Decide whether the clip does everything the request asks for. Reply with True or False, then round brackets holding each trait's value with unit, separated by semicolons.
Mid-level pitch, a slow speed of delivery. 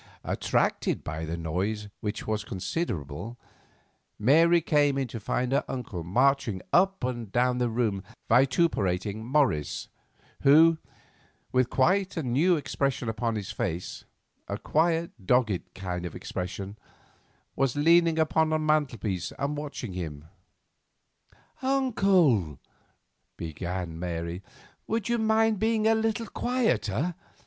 False (125 Hz; 120 wpm)